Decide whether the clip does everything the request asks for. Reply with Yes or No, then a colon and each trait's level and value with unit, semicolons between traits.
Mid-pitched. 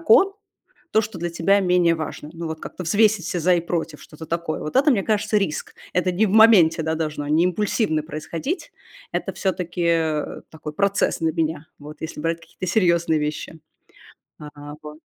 Yes: medium, 170 Hz